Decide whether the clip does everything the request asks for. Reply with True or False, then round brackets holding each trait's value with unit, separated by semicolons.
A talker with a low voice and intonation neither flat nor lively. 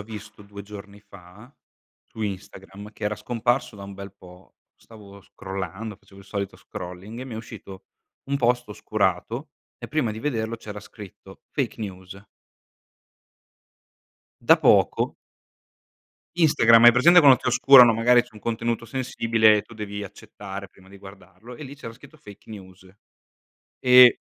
True (105 Hz; 3.4 semitones)